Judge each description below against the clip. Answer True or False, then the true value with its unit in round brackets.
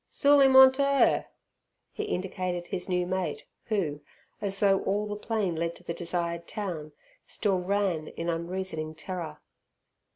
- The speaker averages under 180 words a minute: True (155 wpm)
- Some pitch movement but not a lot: True (3.4 semitones)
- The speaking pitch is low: False (185 Hz)